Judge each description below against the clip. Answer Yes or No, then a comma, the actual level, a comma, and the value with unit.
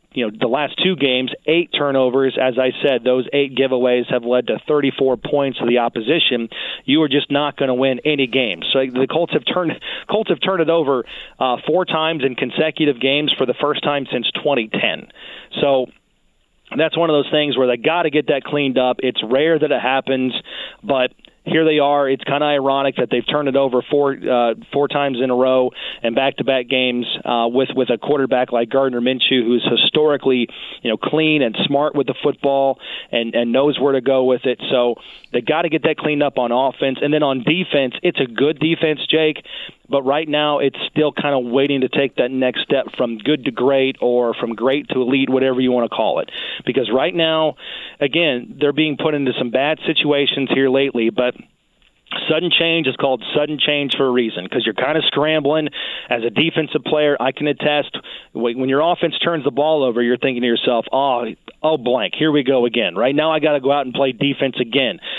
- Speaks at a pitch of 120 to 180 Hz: Yes, low, 135 Hz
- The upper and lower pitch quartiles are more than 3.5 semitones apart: No, average, 2.7 semitones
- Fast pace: Yes, fast, 215 wpm